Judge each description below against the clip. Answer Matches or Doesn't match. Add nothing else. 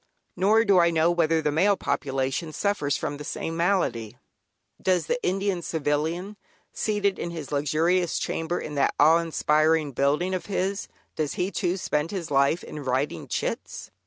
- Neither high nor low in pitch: Matches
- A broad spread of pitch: Doesn't match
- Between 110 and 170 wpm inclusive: Matches